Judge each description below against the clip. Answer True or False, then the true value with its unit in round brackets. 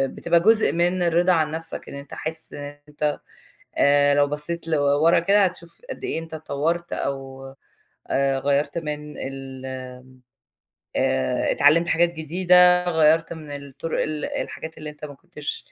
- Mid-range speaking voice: True (155 Hz)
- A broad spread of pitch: False (3.1 semitones)